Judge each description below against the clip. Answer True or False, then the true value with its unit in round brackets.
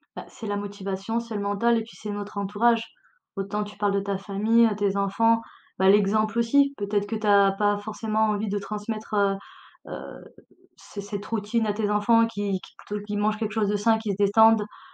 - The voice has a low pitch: False (210 Hz)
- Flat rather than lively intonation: True (1.6 semitones)